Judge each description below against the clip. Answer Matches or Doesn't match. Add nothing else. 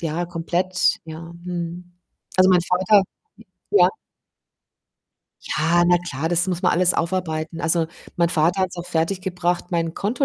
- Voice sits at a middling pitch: Matches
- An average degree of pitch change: Doesn't match